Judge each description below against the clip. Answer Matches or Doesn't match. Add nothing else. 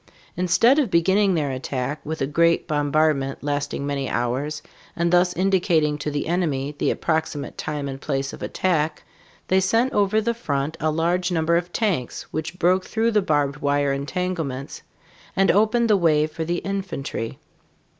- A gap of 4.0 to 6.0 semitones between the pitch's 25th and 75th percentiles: Matches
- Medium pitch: Matches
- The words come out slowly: Doesn't match